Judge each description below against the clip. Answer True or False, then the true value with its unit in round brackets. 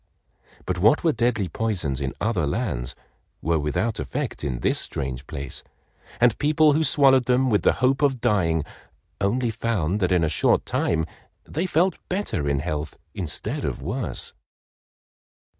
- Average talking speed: True (155 wpm)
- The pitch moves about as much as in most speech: False (8.9 semitones)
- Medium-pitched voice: False (105 Hz)